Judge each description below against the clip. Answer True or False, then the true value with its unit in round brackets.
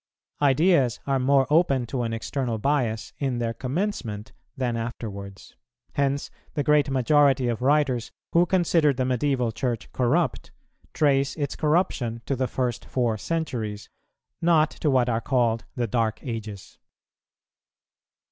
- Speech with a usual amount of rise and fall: True (3.8 semitones)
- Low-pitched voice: True (130 Hz)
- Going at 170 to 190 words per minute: False (135 wpm)